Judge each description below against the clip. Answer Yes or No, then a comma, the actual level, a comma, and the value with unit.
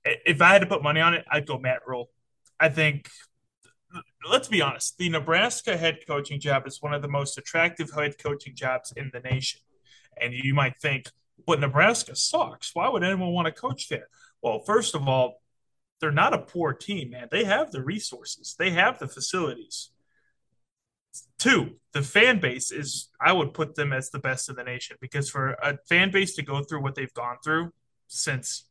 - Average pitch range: Yes, average, 3.8 semitones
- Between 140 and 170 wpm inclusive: No, average, 200 wpm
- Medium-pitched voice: Yes, medium, 145 Hz